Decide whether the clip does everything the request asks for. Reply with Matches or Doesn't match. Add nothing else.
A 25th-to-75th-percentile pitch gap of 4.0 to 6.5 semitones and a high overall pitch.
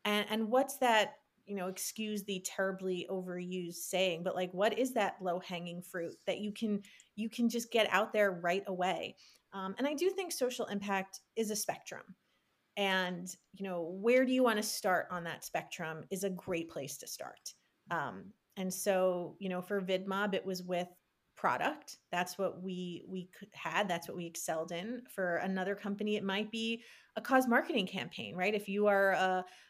Doesn't match